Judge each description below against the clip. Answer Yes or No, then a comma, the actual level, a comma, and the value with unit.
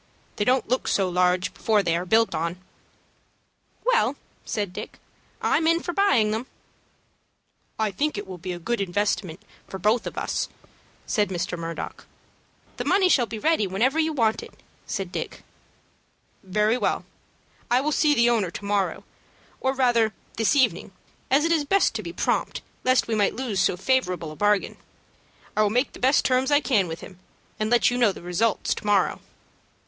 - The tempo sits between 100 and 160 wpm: No, average, 180 wpm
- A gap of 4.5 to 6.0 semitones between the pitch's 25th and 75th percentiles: Yes, wide, 5.4 semitones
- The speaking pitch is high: Yes, high, 215 Hz